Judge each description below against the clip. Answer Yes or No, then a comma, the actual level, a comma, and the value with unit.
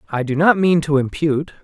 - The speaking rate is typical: No, fast, 220 wpm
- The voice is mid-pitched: Yes, medium, 145 Hz